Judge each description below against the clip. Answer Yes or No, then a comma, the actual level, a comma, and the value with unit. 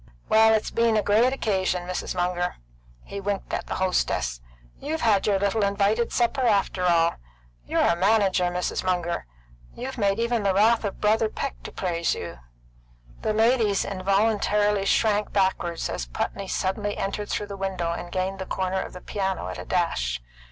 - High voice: Yes, high, 195 Hz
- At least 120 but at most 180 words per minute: Yes, average, 175 wpm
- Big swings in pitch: No, average, 2.8 semitones